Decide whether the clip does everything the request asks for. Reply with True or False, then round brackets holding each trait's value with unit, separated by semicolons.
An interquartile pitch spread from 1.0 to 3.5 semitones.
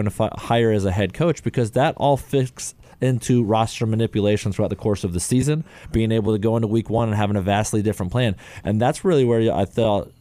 True (3.0 semitones)